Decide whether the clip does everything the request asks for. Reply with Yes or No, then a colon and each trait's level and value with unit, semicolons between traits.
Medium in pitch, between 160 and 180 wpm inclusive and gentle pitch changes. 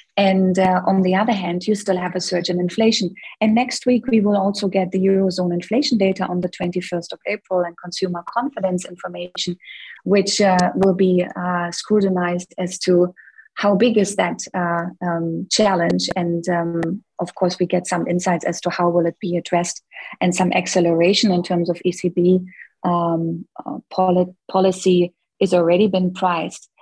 Yes: medium, 180 Hz; average, 170 wpm; narrow, 1.6 semitones